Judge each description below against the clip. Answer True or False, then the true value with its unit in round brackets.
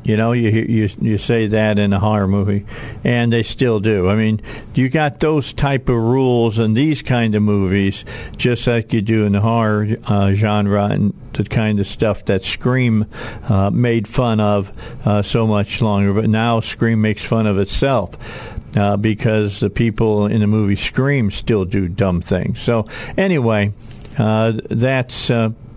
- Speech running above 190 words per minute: False (175 wpm)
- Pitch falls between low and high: False (110 Hz)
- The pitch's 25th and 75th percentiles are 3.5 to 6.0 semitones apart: False (2.4 semitones)